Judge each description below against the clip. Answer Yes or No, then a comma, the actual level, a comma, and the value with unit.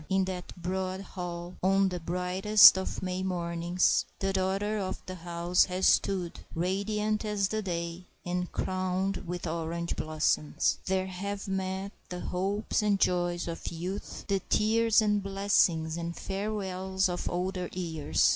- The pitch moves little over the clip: Yes, narrow, 1.9 semitones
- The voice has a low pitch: No, medium, 185 Hz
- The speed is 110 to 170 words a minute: Yes, average, 145 wpm